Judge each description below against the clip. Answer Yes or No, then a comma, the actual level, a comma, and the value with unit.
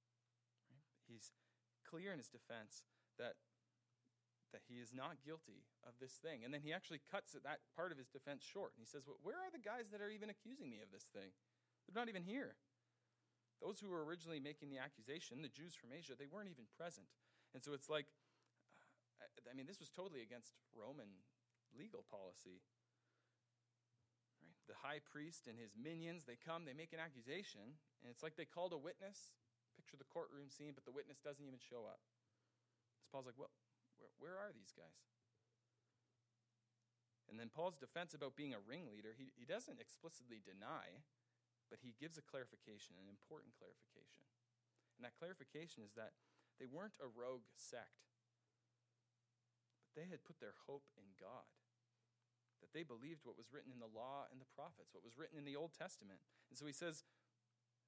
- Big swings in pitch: No, average, 4.5 semitones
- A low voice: Yes, low, 125 Hz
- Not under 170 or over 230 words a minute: Yes, average, 180 wpm